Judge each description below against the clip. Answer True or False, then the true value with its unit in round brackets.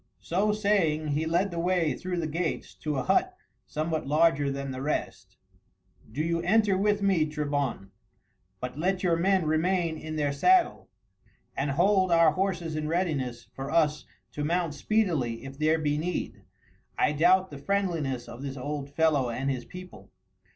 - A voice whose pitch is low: False (160 Hz)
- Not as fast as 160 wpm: False (165 wpm)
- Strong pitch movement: False (4.0 semitones)